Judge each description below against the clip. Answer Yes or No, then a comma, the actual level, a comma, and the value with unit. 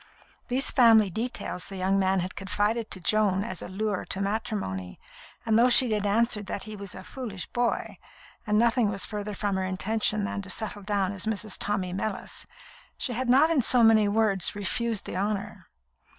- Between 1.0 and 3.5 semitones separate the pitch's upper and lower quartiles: Yes, narrow, 2.5 semitones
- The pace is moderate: Yes, average, 190 wpm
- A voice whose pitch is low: No, high, 210 Hz